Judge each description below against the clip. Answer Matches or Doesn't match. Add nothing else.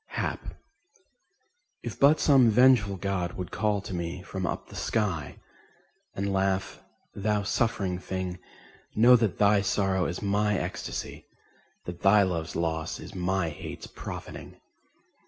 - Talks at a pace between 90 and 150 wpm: Matches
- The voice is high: Doesn't match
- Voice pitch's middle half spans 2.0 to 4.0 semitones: Matches